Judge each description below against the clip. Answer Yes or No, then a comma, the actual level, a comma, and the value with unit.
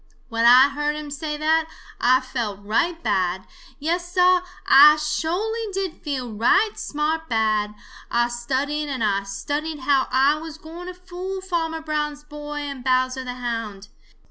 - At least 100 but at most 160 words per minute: Yes, average, 155 wpm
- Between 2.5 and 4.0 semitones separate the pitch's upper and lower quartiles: No, average, 5.0 semitones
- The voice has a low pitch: No, very high, 295 Hz